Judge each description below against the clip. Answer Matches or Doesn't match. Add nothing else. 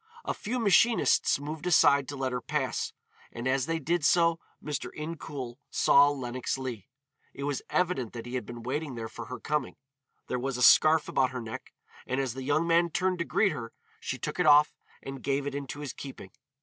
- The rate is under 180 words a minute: Doesn't match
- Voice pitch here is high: Doesn't match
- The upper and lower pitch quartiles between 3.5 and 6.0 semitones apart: Matches